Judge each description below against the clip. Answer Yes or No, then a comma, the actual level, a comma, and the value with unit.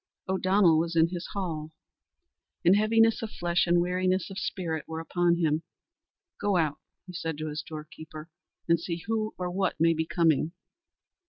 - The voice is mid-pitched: Yes, medium, 170 Hz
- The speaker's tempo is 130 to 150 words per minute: No, average, 165 wpm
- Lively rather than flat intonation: No, narrow, 2.5 semitones